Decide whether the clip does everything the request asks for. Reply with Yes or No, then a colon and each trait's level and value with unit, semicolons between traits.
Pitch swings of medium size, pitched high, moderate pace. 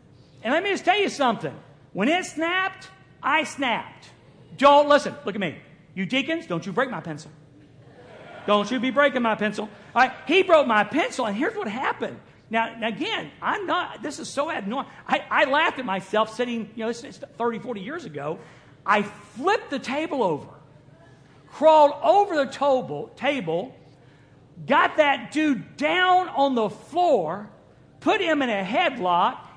No: wide, 8.4 semitones; high, 235 Hz; average, 170 wpm